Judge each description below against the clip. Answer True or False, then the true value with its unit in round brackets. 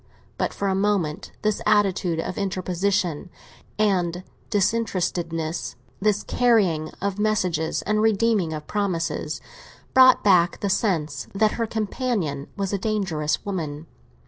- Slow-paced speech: True (120 wpm)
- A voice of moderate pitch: False (195 Hz)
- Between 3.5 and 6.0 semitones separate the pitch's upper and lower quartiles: True (4.1 semitones)